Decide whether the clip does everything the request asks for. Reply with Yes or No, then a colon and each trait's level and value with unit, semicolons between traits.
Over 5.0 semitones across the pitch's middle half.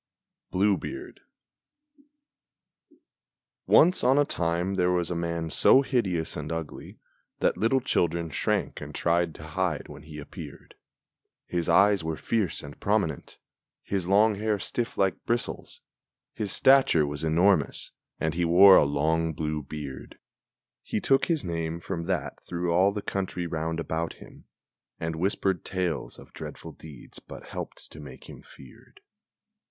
No: average, 3.8 semitones